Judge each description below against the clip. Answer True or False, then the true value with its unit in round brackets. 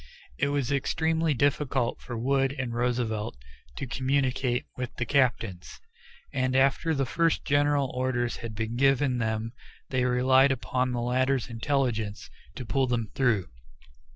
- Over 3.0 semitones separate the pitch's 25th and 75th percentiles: False (2.4 semitones)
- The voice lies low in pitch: True (130 Hz)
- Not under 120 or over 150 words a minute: True (140 wpm)